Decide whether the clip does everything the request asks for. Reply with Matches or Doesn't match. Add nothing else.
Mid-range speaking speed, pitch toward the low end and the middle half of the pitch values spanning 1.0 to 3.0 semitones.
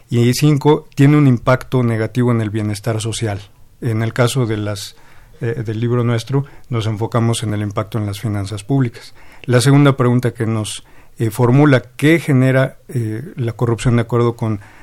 Matches